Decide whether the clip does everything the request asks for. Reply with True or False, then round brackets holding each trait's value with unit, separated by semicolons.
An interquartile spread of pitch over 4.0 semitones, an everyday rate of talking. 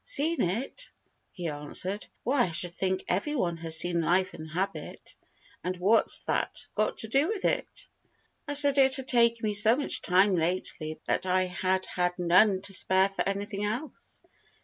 True (4.6 semitones; 175 wpm)